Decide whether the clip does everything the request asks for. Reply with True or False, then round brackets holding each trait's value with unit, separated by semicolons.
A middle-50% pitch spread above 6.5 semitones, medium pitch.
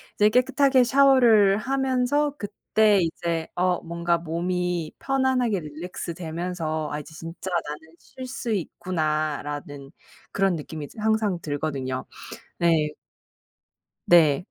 False (5.8 semitones; 175 Hz)